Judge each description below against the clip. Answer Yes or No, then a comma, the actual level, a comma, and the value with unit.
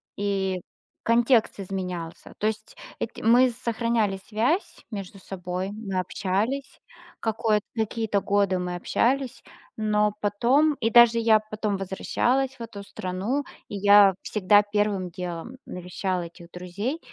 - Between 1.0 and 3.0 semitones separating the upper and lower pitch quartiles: No, average, 3.4 semitones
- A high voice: Yes, high, 210 Hz